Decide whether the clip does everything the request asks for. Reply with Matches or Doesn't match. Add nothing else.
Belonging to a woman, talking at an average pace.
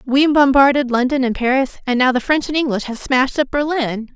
Doesn't match